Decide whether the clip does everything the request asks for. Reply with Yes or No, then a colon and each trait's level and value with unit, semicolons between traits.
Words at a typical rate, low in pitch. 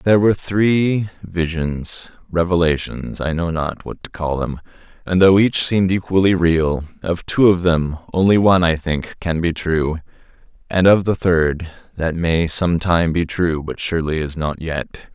Yes: average, 160 wpm; very low, 85 Hz